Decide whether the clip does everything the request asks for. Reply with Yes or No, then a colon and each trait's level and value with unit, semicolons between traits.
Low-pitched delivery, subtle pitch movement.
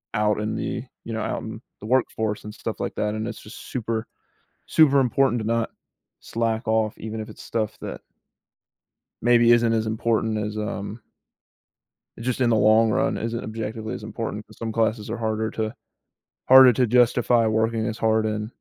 Yes: low, 110 Hz; narrow, 1.4 semitones